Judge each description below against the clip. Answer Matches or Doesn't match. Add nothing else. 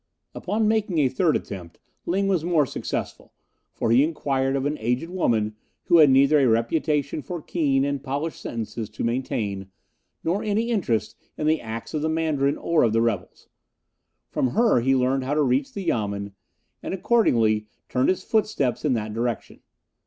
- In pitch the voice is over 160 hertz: Doesn't match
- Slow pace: Doesn't match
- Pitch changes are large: Matches